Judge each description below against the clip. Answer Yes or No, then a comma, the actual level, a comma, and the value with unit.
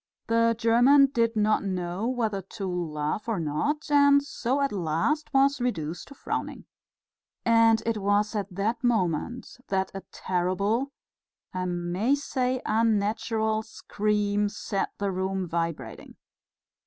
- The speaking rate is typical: No, slow, 130 wpm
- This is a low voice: No, high, 215 Hz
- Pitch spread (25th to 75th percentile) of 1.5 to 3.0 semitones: No, average, 4.2 semitones